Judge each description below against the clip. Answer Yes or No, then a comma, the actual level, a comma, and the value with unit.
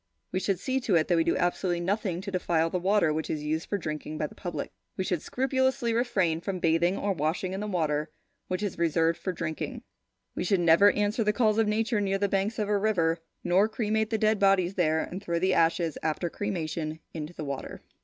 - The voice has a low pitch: No, medium, 185 Hz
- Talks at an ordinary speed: No, fast, 225 wpm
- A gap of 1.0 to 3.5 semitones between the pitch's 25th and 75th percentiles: No, average, 4.1 semitones